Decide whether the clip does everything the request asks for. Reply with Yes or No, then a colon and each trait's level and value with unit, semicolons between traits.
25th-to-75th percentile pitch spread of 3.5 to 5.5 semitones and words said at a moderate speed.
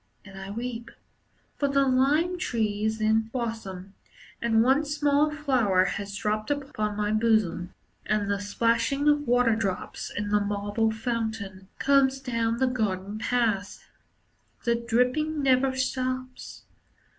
No: average, 4.0 semitones; slow, 130 wpm